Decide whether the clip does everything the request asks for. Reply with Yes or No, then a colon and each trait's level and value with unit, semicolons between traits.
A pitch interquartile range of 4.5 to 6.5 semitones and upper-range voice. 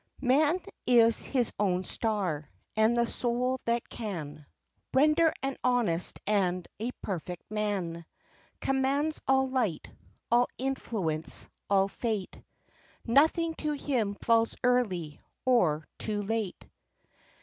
Yes: wide, 5.4 semitones; high, 230 Hz